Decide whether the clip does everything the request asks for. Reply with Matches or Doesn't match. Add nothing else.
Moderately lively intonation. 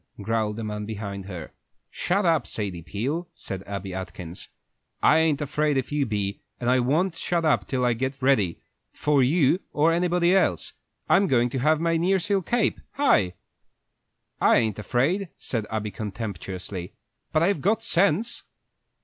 Doesn't match